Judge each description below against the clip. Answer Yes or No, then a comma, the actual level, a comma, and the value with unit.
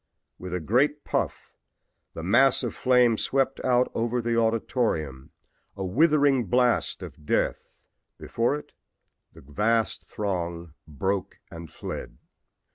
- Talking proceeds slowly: Yes, slow, 120 wpm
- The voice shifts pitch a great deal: Yes, wide, 6.4 semitones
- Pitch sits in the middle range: No, low, 115 Hz